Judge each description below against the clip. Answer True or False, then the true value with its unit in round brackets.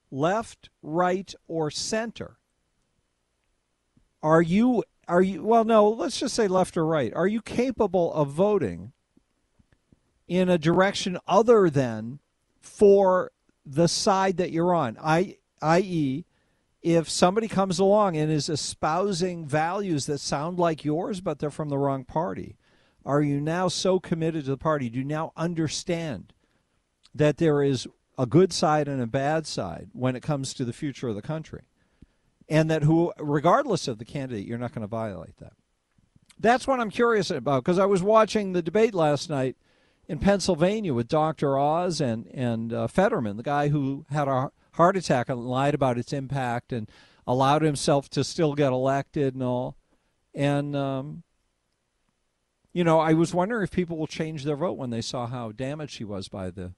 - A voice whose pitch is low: False (155 Hz)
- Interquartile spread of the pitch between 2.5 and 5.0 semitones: False (5.5 semitones)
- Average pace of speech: True (170 wpm)